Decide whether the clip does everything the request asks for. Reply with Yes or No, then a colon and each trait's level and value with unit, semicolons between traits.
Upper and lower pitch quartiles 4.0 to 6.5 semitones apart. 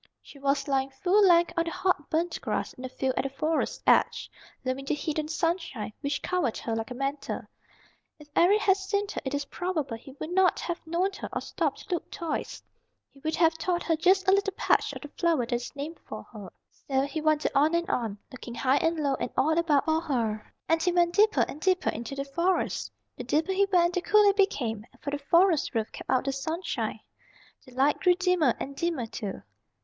Yes: average, 4.5 semitones